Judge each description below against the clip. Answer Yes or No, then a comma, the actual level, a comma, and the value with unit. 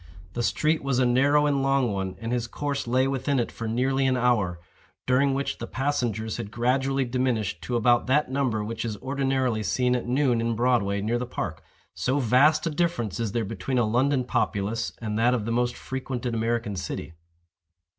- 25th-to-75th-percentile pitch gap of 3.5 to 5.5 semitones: No, average, 2.8 semitones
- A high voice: No, low, 125 Hz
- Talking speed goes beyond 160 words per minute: Yes, average, 190 wpm